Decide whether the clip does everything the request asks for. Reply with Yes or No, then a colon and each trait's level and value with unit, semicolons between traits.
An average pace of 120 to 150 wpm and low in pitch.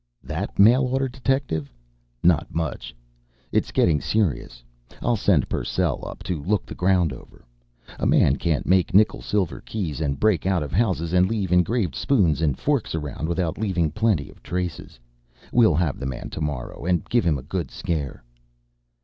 No: average, 175 wpm; very low, 90 Hz